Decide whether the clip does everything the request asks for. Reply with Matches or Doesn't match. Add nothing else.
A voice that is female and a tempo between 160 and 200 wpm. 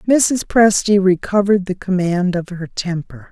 Doesn't match